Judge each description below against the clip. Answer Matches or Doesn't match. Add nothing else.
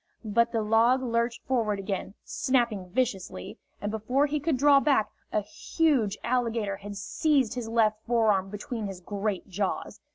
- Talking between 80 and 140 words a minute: Doesn't match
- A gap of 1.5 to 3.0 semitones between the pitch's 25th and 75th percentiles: Doesn't match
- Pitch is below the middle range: Doesn't match